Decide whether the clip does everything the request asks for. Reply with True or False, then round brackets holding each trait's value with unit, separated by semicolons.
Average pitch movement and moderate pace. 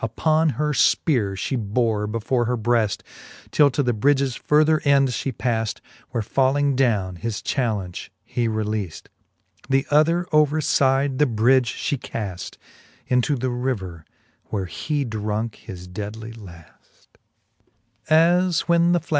False (4.5 semitones; 125 wpm)